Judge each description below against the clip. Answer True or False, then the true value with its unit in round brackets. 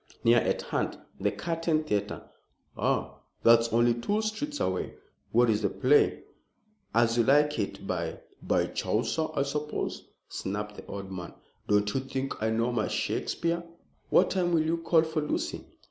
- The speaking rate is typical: True (165 wpm)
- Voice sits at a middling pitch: False (120 Hz)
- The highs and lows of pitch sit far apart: True (7.1 semitones)